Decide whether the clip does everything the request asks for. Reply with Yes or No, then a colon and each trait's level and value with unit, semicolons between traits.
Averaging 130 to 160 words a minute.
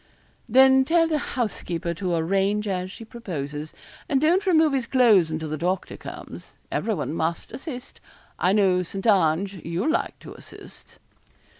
Yes: average, 150 wpm